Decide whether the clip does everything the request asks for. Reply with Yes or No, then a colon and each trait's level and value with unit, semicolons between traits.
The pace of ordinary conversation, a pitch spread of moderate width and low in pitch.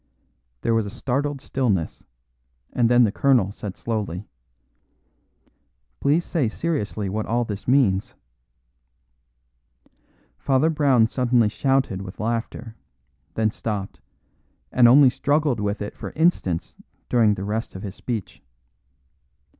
No: slow, 120 wpm; average, 4.5 semitones; low, 115 Hz